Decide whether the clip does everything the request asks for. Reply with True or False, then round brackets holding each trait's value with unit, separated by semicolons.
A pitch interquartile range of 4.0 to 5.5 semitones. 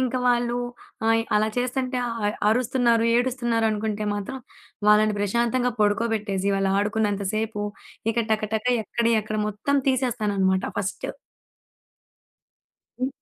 False (2.7 semitones)